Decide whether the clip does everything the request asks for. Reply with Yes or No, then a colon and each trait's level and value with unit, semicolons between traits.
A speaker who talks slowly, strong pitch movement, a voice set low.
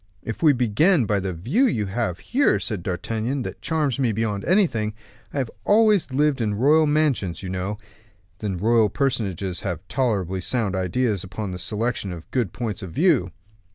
No: average, 170 wpm; wide, 6.4 semitones; low, 110 Hz